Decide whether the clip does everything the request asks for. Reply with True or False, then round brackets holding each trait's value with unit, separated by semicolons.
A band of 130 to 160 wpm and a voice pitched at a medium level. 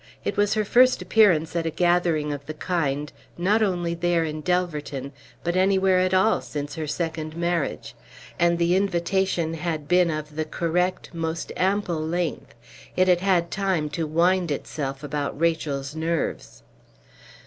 True (155 wpm; 170 Hz)